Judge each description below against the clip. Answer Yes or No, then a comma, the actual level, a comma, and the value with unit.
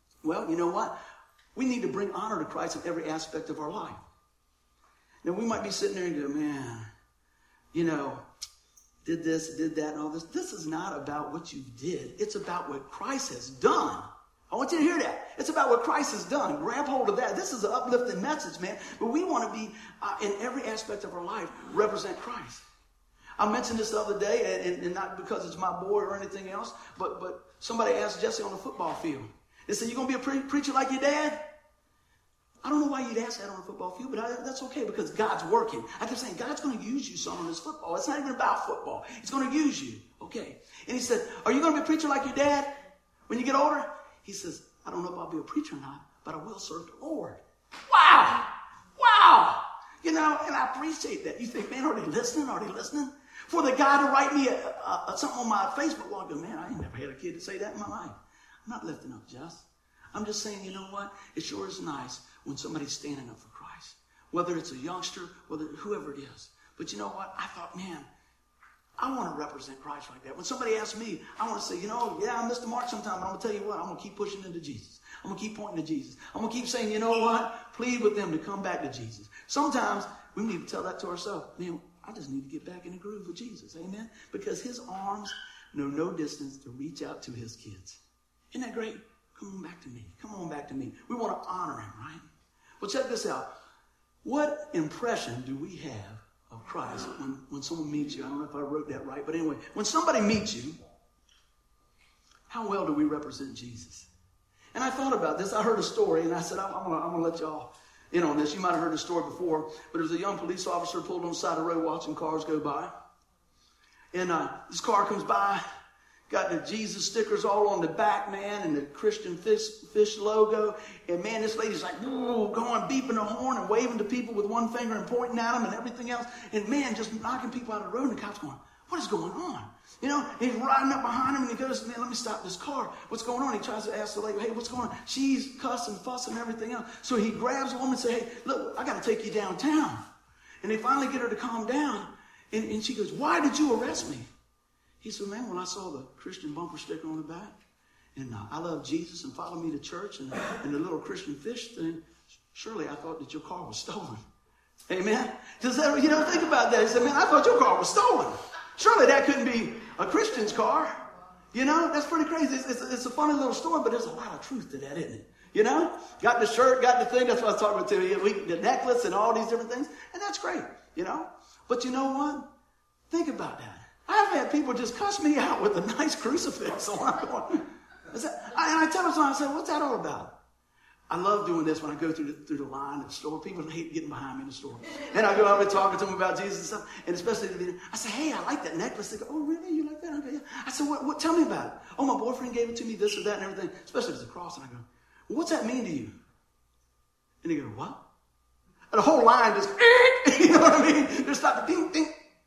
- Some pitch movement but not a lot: No, wide, 8.7 semitones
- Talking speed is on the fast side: Yes, fast, 250 wpm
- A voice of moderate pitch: No, high, 220 Hz